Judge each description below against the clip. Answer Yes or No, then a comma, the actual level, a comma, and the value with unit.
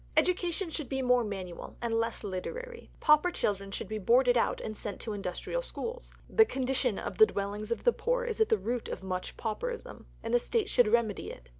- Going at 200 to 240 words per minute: Yes, fast, 205 wpm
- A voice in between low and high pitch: No, high, 240 Hz